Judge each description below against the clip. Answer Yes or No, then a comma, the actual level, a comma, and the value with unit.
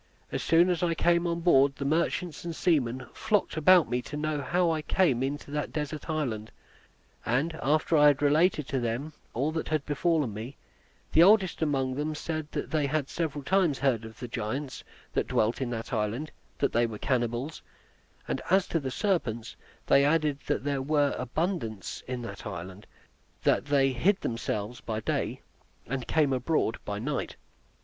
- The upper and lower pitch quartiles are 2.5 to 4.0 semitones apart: No, average, 4.6 semitones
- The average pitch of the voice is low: No, medium, 145 Hz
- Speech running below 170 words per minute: No, average, 175 wpm